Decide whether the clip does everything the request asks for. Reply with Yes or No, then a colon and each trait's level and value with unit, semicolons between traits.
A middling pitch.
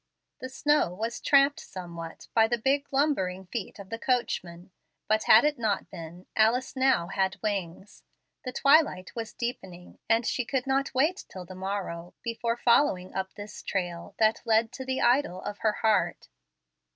No: high, 220 Hz